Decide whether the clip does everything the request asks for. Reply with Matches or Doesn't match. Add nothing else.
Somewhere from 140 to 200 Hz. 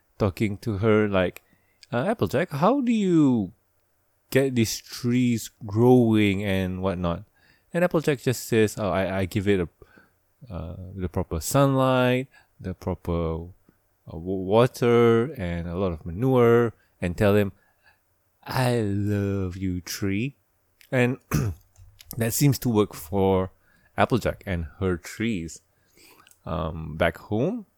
Doesn't match